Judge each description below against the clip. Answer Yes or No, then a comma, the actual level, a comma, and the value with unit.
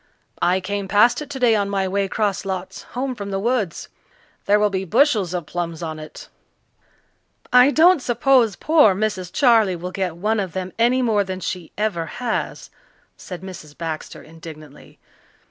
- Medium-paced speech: Yes, average, 165 wpm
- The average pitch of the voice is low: No, high, 200 Hz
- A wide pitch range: No, average, 4.5 semitones